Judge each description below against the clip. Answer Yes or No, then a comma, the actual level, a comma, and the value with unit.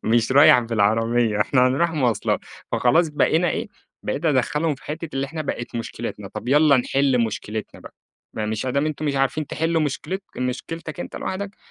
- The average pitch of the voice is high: No, low, 135 Hz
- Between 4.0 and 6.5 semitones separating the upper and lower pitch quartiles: Yes, average, 4.4 semitones